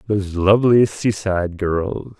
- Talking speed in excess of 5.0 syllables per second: No, 4.6 syllables/s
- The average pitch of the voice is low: Yes, low, 100 Hz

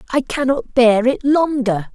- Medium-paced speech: Yes, average, 155 wpm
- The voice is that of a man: Yes, male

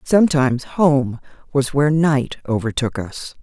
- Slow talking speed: Yes, slow, 125 wpm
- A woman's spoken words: Yes, female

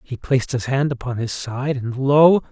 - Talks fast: Yes, fast, 215 wpm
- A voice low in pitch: Yes, low, 130 Hz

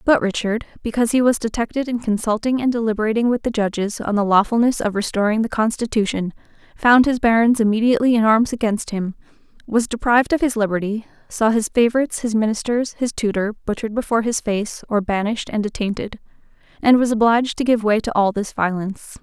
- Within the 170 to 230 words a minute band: Yes, average, 180 wpm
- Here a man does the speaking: No, female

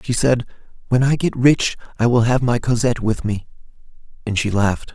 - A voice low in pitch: Yes, low, 120 Hz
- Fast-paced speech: No, average, 195 wpm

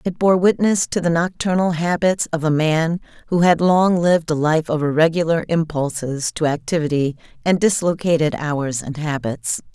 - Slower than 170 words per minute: Yes, average, 160 wpm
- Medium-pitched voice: Yes, medium, 160 Hz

